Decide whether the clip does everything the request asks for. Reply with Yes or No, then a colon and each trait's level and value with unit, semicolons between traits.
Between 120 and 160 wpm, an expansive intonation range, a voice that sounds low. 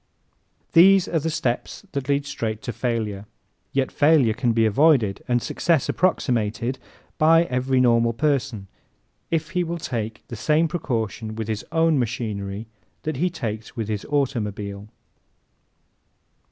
Yes: average, 140 wpm; wide, 5.8 semitones; low, 125 Hz